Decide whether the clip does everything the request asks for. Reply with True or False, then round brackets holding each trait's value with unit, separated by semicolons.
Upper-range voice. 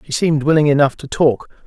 False (145 Hz)